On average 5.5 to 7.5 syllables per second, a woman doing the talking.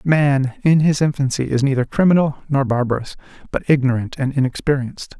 No: 5.7 syllables/s; male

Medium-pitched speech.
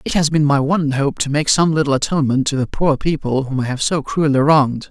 Yes: medium, 145 Hz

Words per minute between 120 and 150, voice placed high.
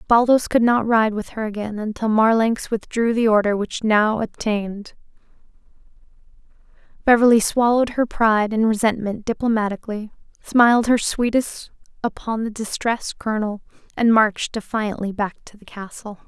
Yes: slow, 135 wpm; high, 220 Hz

